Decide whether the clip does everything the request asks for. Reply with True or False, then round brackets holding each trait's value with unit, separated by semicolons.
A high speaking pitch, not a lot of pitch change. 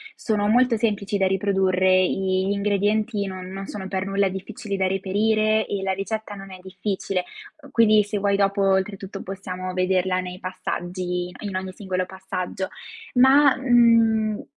True (195 Hz; 2.1 semitones)